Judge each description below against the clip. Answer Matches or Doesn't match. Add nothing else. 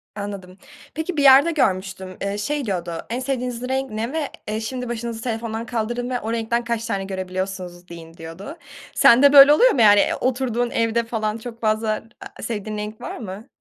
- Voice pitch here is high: Matches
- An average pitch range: Matches